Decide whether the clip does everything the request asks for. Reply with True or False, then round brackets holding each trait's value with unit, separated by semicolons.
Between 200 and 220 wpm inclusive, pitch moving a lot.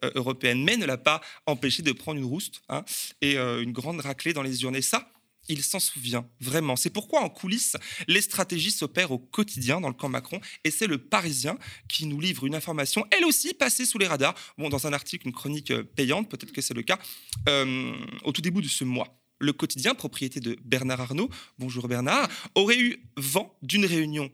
True (205 wpm; 6.0 semitones)